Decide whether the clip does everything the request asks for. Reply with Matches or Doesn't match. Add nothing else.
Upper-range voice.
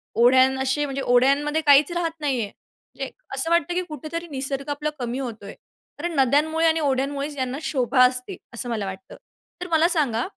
Matches